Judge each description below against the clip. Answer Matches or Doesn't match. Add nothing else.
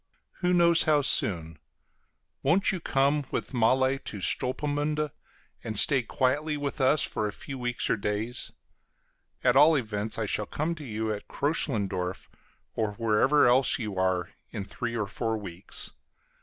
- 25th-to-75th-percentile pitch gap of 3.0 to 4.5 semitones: Doesn't match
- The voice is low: Matches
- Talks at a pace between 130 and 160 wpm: Matches